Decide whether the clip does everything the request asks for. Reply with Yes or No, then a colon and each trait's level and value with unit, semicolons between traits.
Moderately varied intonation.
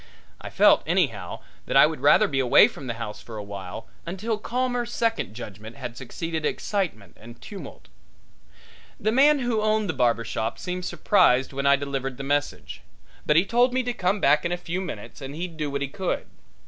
No: wide, 8.8 semitones